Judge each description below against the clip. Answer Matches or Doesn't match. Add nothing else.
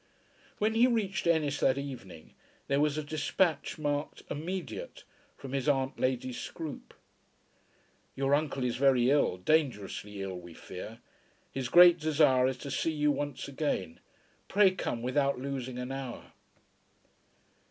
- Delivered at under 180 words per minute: Matches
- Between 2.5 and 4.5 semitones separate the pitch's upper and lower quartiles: Matches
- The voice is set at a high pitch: Doesn't match